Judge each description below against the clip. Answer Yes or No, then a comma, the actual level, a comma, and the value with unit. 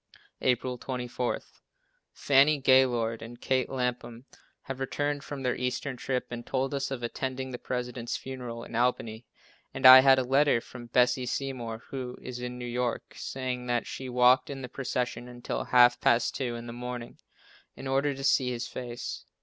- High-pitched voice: No, low, 125 Hz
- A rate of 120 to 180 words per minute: Yes, average, 175 wpm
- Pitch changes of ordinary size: No, narrow, 1.5 semitones